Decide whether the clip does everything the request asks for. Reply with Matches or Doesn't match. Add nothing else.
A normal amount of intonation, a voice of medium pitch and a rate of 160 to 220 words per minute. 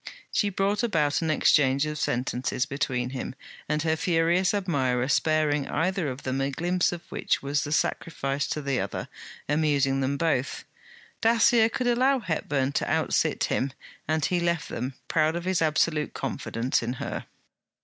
Matches